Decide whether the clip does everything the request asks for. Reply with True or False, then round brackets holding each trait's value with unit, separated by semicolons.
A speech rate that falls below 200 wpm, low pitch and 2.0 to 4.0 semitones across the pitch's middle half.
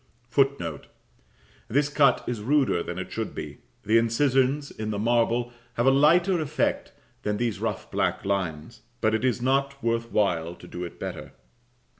False (165 wpm; 120 Hz; 4.8 semitones)